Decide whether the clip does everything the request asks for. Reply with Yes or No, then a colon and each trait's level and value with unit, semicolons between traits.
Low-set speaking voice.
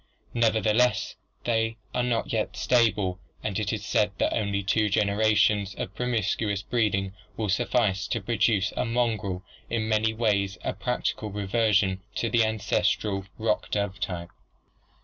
Yes: low, 105 Hz